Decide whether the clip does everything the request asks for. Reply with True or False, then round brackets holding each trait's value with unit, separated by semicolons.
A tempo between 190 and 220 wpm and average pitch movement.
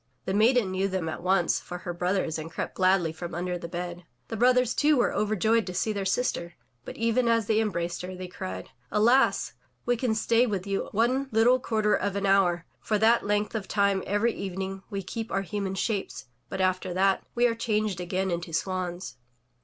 True (205 wpm; 3.6 semitones)